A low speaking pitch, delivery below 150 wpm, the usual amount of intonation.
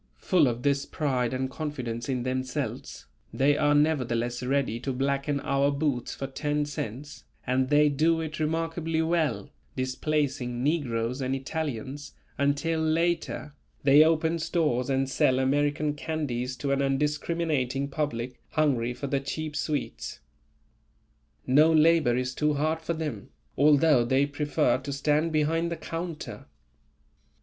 No: medium, 145 Hz; slow, 135 wpm; average, 3.1 semitones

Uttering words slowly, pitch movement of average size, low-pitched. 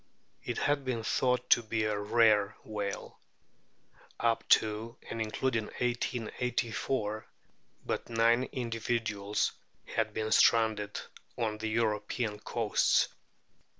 No: slow, 105 wpm; narrow, 1.8 semitones; low, 115 Hz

